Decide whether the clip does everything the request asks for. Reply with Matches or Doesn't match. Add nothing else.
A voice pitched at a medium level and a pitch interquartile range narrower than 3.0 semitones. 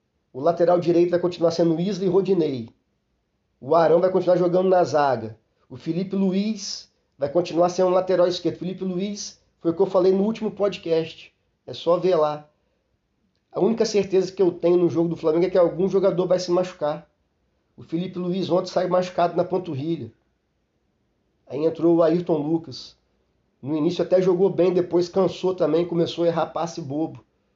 Matches